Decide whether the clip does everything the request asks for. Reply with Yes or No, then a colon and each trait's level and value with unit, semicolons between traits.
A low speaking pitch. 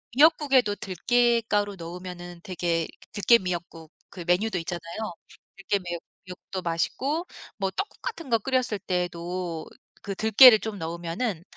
No: high, 190 Hz